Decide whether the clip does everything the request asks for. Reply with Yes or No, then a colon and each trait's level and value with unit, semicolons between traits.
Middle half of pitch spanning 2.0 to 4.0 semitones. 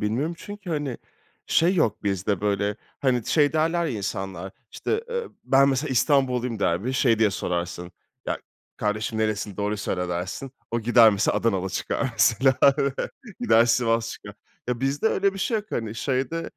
No: wide, 5.5 semitones